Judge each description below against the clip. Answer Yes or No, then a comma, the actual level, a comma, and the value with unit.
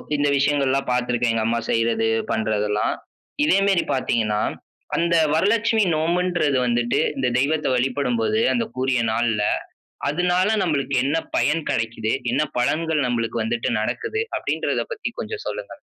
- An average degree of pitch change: No, wide, 5.7 semitones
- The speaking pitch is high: No, low, 130 Hz